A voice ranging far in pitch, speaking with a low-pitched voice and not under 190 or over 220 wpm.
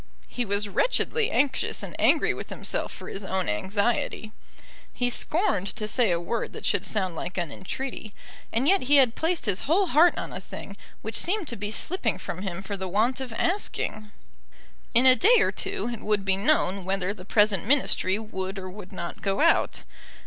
No: wide, 5.8 semitones; high, 215 Hz; average, 195 wpm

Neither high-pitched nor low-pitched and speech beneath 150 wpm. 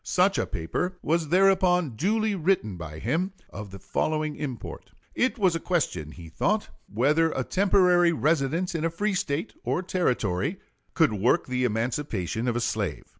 No: medium, 155 Hz; average, 165 wpm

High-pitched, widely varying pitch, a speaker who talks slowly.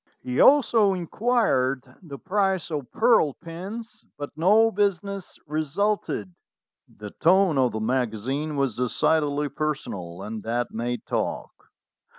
No: medium, 150 Hz; wide, 7.9 semitones; slow, 120 wpm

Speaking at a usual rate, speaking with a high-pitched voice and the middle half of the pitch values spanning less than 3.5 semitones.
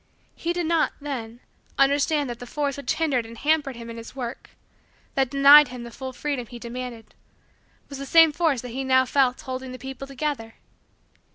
Yes: average, 190 wpm; very high, 265 Hz; average, 2.9 semitones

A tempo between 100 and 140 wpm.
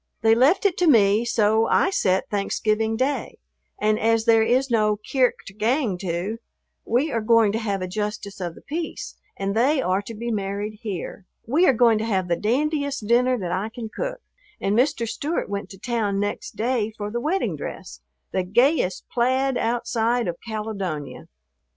No: average, 180 wpm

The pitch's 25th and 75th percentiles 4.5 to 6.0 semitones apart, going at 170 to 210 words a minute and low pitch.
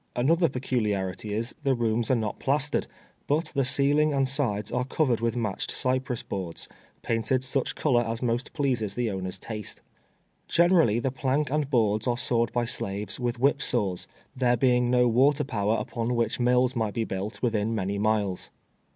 No: average, 3.4 semitones; average, 175 wpm; low, 120 Hz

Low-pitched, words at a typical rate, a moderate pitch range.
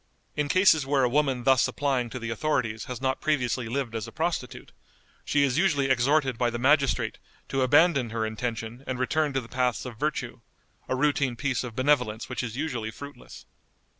Yes: low, 130 Hz; average, 190 wpm; average, 3.1 semitones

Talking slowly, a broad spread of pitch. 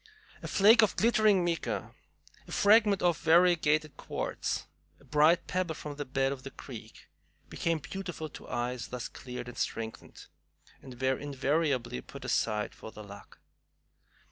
No: average, 145 wpm; wide, 5.8 semitones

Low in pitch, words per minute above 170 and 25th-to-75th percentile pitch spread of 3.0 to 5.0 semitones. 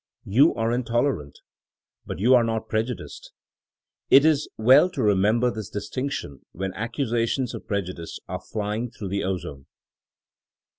No: low, 115 Hz; average, 145 wpm; average, 3.9 semitones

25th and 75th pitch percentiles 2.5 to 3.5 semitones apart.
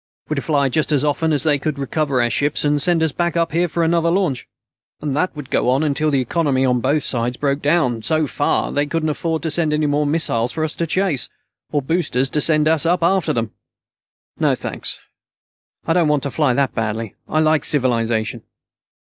Yes: average, 3.2 semitones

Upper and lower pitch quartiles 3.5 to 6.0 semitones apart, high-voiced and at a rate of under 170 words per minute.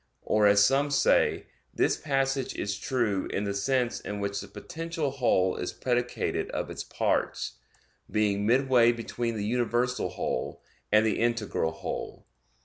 No: average, 4.3 semitones; low, 120 Hz; average, 145 wpm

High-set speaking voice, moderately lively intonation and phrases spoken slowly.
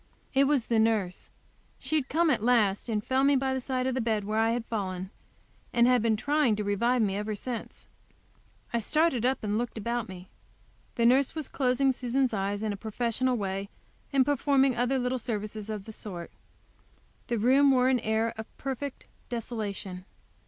No: high, 235 Hz; average, 3.6 semitones; average, 190 wpm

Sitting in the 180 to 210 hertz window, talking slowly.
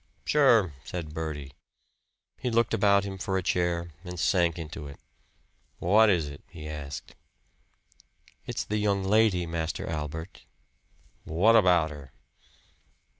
No: very low, 85 Hz; slow, 125 wpm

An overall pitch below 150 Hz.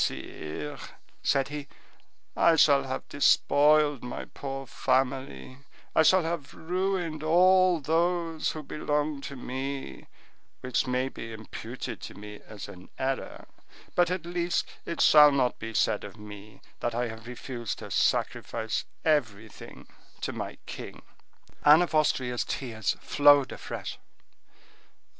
Yes: medium, 140 Hz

